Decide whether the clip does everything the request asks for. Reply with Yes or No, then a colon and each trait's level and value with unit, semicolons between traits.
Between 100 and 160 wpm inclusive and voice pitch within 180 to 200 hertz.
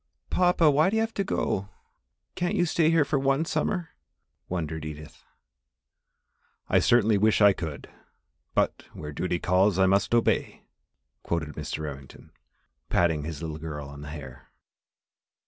No: average, 145 wpm; very low, 95 Hz